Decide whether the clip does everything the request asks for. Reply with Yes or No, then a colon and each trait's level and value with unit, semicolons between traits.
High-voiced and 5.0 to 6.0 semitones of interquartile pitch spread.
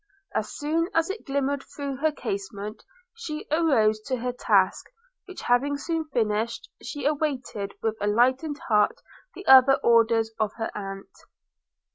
Yes: very high, 255 Hz; average, 5.3 semitones